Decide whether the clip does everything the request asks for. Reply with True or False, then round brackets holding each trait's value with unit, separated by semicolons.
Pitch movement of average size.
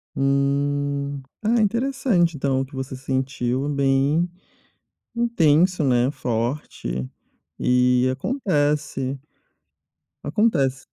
True (4.1 semitones)